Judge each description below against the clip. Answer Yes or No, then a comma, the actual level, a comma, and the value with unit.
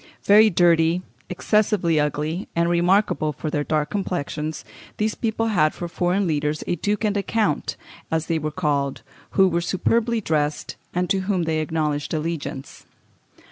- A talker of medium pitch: Yes, medium, 170 Hz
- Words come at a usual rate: Yes, average, 155 wpm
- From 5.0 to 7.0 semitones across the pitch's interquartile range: No, average, 4.3 semitones